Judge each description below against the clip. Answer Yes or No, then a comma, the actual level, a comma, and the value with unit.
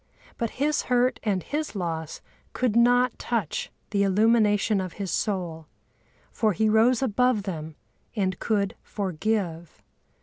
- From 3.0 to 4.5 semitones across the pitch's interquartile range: Yes, average, 4.1 semitones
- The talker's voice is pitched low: No, high, 210 Hz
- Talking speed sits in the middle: No, slow, 130 wpm